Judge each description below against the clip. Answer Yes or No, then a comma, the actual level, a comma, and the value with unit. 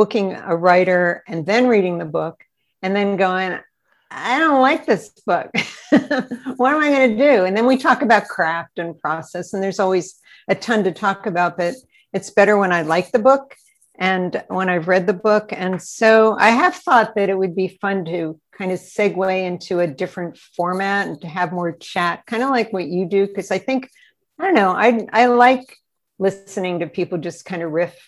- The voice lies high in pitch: Yes, high, 195 Hz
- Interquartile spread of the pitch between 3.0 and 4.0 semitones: No, average, 4.4 semitones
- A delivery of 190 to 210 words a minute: Yes, fast, 205 wpm